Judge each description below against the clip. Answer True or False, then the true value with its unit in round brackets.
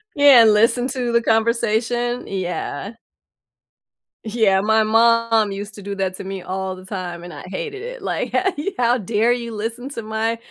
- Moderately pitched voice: False (225 Hz)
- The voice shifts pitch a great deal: False (3.4 semitones)